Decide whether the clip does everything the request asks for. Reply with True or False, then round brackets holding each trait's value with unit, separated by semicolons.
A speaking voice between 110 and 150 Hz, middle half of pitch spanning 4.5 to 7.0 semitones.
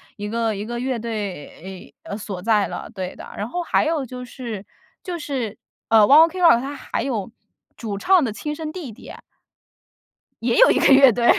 False (235 Hz; 5.5 semitones)